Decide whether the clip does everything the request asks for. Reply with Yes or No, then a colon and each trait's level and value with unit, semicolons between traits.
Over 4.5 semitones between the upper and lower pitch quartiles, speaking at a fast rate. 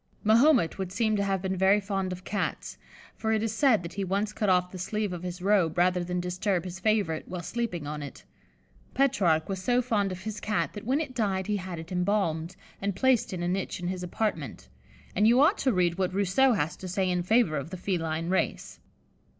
No: average, 3.1 semitones; fast, 225 wpm